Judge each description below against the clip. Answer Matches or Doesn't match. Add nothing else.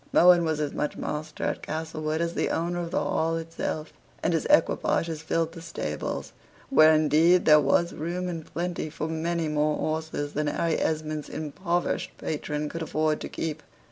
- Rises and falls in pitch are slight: Matches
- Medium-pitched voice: Matches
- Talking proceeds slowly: Doesn't match